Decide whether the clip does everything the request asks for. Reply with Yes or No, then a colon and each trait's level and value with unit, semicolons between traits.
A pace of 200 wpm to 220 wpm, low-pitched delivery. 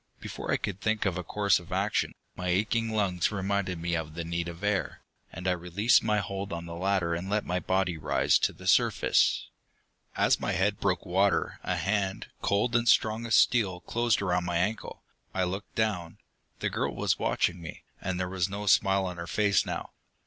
Yes: fast, 205 wpm; very low, 95 Hz